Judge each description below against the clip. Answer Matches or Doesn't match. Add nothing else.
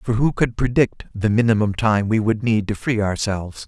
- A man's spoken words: Matches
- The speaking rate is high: Matches